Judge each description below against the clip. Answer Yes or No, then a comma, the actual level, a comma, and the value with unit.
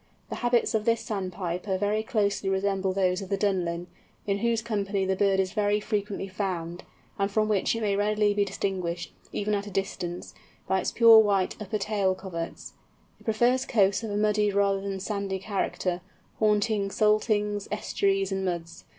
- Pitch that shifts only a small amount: Yes, narrow, 1.8 semitones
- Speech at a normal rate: Yes, average, 175 wpm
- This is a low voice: No, high, 200 Hz